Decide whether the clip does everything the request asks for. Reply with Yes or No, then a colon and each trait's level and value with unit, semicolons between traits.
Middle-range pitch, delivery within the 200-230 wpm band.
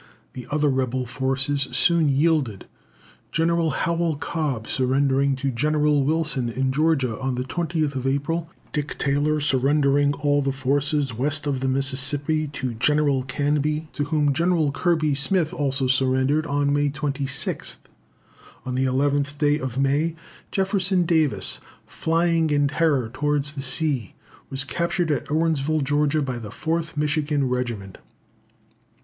No: medium, 145 Hz; slow, 135 wpm